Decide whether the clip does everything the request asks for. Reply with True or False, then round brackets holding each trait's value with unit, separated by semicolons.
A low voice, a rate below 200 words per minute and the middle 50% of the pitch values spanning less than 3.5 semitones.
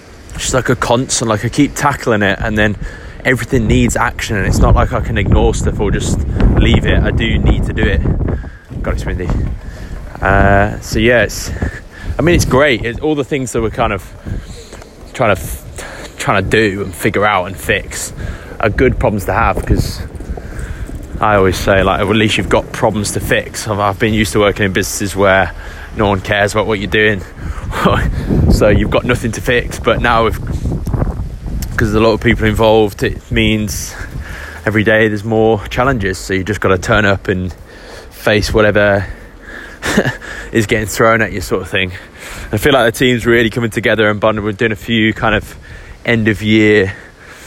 True (105 Hz; 190 wpm; 2.8 semitones)